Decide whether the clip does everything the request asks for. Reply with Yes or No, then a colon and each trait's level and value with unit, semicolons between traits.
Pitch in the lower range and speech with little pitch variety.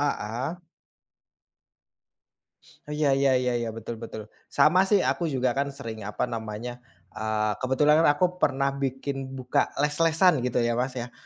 No: low, 130 Hz; average, 3.5 semitones